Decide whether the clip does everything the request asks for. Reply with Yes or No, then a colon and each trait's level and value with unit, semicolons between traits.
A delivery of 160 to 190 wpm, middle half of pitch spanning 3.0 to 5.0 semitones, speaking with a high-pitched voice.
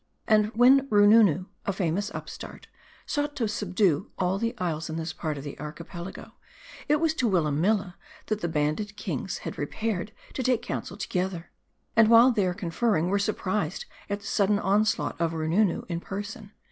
Yes: average, 170 wpm; average, 4.1 semitones; high, 200 Hz